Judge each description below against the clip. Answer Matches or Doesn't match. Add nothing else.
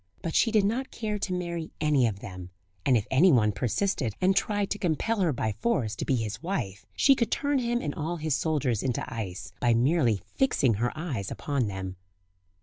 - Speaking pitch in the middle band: Matches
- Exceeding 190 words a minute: Matches